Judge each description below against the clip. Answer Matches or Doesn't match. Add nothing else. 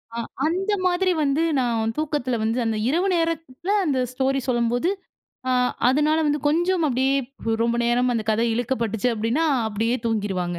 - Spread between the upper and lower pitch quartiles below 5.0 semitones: Doesn't match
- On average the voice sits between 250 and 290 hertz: Matches